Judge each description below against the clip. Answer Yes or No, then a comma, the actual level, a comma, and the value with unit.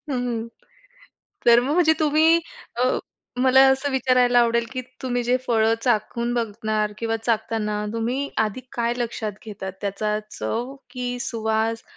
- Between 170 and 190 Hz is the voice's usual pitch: No, high, 235 Hz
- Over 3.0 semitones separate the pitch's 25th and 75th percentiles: No, narrow, 2.4 semitones